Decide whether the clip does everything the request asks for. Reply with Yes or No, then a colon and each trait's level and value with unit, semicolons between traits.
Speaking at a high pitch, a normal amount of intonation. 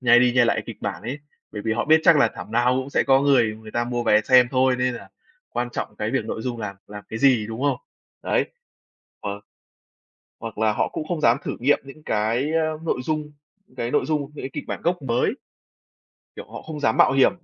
No: low, 125 Hz; average, 3.9 semitones